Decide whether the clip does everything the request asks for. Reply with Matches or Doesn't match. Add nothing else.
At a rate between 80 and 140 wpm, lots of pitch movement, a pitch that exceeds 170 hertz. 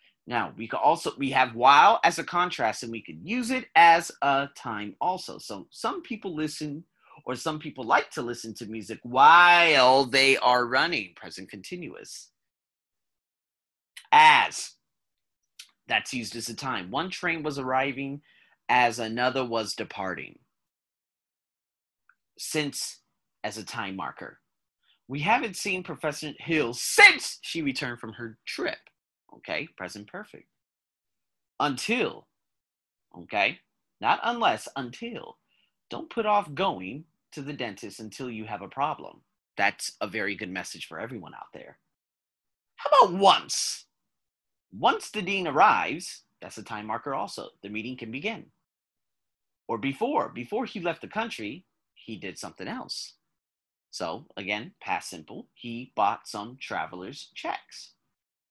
Doesn't match